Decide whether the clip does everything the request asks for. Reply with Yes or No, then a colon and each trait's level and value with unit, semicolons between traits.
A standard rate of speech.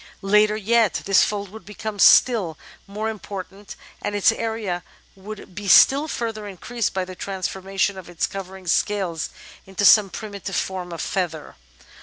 Yes: average, 150 wpm